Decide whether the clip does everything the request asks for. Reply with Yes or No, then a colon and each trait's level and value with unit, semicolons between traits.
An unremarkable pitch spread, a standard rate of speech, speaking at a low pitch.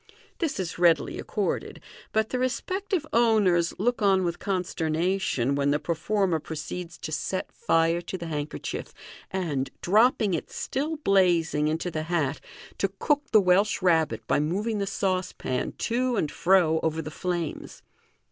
No: average, 4.4 semitones; average, 145 wpm; medium, 180 Hz